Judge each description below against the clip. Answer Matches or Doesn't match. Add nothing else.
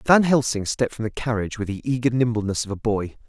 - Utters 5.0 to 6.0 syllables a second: Doesn't match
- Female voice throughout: Doesn't match